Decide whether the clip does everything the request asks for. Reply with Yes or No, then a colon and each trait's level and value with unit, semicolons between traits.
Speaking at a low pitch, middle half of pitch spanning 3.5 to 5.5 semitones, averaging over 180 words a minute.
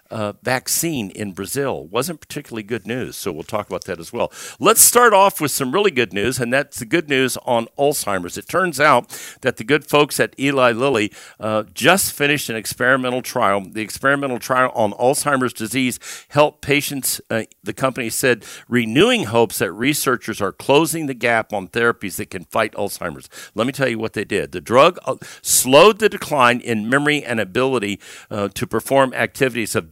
Yes: low, 125 Hz; average, 4.2 semitones; average, 190 wpm